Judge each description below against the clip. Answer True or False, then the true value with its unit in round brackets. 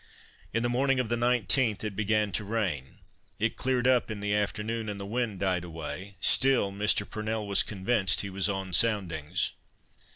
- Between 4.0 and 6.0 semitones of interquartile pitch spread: False (3.2 semitones)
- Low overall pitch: True (105 Hz)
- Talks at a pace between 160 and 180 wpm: True (175 wpm)